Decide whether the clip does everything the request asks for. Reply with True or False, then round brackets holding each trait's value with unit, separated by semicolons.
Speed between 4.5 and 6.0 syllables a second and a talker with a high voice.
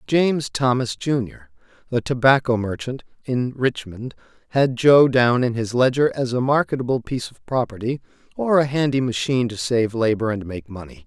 False (5.1 syllables/s; 120 Hz)